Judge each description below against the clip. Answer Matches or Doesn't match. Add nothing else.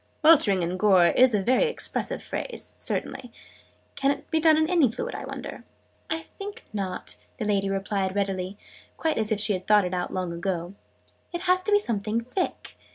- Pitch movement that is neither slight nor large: Doesn't match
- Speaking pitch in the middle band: Doesn't match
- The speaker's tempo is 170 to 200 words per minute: Matches